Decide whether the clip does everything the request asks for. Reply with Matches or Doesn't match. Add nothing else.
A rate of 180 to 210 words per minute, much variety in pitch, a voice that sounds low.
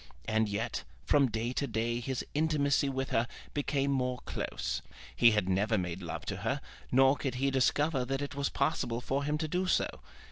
Doesn't match